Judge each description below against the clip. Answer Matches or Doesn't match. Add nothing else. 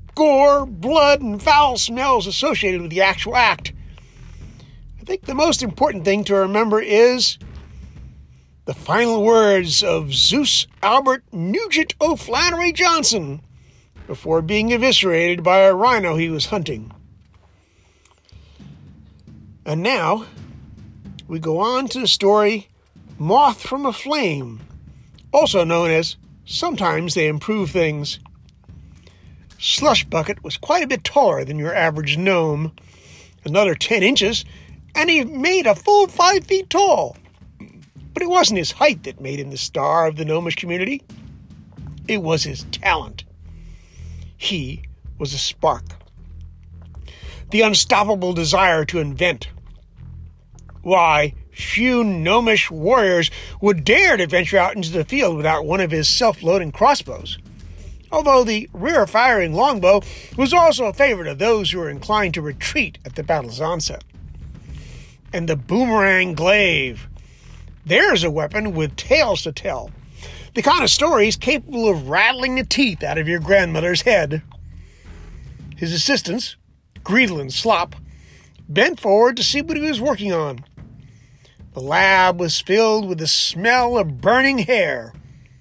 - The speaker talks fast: Doesn't match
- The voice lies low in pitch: Doesn't match